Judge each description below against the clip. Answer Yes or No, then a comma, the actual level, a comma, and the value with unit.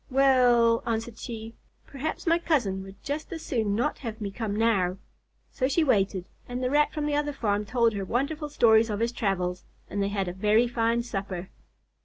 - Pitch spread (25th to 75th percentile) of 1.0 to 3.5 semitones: No, average, 4.7 semitones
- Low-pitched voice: No, high, 230 Hz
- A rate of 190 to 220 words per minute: Yes, average, 200 wpm